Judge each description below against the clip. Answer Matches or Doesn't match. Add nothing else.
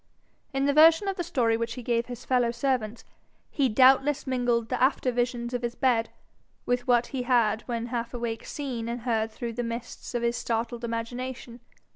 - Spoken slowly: Doesn't match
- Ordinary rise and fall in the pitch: Doesn't match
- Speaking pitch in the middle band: Doesn't match